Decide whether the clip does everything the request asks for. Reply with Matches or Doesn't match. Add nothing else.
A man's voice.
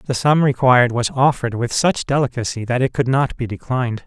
Matches